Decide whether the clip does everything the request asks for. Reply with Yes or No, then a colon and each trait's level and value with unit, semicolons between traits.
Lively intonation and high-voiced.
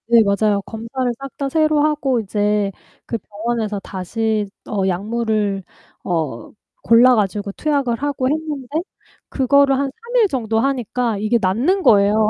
No: average, 4.7 semitones; high, 225 Hz